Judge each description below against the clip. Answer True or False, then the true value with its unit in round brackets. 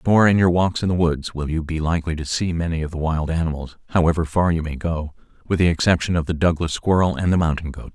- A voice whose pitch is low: True (85 Hz)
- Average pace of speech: False (255 wpm)